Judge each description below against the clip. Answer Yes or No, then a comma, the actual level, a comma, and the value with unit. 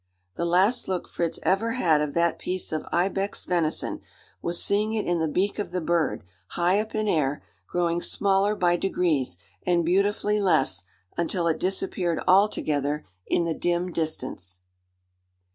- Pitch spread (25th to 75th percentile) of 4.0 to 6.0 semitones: No, average, 3.3 semitones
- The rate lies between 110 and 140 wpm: No, average, 155 wpm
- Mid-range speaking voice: Yes, medium, 175 Hz